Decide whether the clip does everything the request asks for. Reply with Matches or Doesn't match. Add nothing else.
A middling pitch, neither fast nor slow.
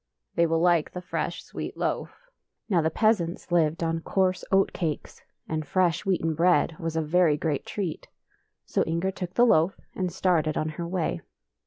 Matches